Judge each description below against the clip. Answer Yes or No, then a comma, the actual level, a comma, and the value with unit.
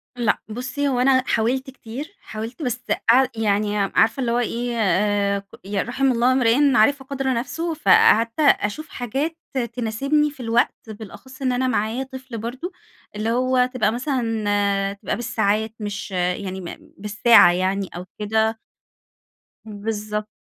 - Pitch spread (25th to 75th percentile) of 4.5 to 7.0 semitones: No, average, 3.8 semitones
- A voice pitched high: Yes, high, 230 Hz